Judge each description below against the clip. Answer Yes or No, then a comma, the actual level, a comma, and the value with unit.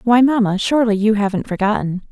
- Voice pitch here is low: No, high, 215 Hz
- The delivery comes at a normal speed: Yes, average, 170 wpm